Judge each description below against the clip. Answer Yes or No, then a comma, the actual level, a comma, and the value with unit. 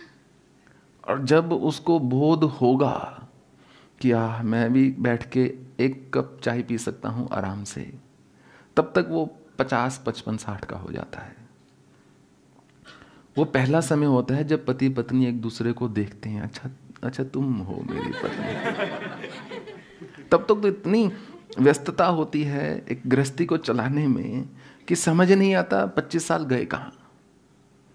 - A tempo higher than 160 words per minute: No, average, 145 wpm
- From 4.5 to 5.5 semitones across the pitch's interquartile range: Yes, average, 5.2 semitones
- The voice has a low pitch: Yes, low, 130 Hz